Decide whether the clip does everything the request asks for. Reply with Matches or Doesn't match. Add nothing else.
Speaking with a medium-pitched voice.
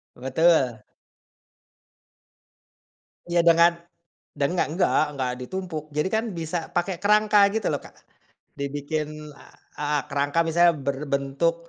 Matches